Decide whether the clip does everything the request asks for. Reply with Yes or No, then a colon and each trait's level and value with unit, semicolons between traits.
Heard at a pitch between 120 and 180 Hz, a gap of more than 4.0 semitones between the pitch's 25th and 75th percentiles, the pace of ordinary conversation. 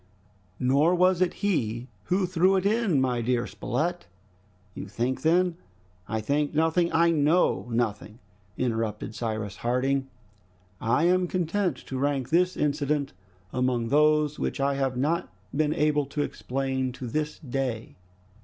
Yes: medium, 140 Hz; average, 5.2 semitones; average, 145 wpm